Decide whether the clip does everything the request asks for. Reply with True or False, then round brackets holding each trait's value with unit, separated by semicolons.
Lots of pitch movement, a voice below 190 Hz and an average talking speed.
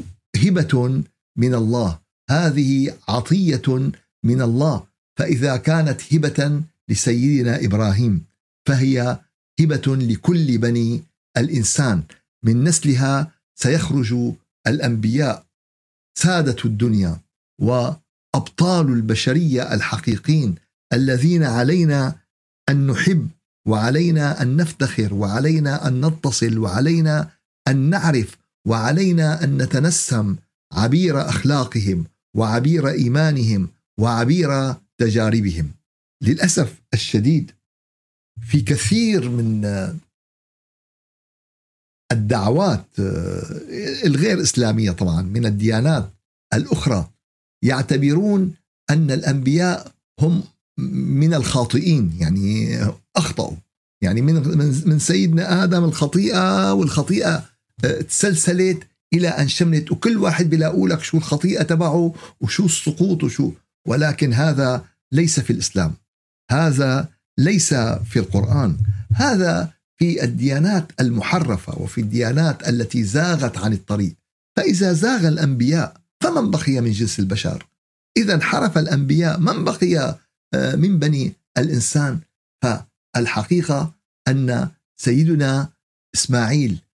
True (5.8 semitones; 135 Hz; 90 wpm)